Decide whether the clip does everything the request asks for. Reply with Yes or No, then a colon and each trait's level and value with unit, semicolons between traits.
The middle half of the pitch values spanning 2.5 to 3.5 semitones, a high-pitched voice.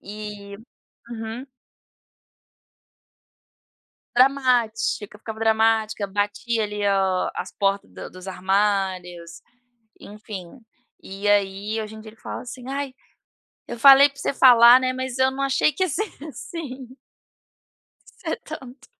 No: average, 4.3 semitones; high, 220 Hz